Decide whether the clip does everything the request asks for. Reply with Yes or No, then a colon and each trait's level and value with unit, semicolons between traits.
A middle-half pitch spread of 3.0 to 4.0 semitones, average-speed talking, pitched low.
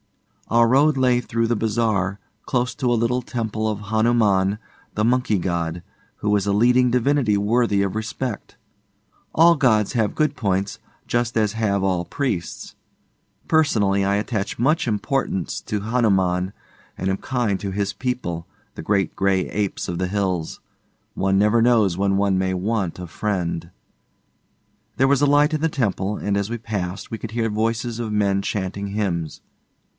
Yes: average, 3.6 semitones; average, 165 wpm; low, 105 Hz